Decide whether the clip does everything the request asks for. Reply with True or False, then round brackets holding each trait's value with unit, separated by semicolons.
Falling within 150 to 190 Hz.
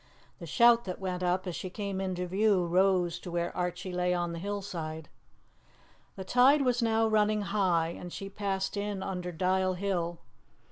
True (185 Hz)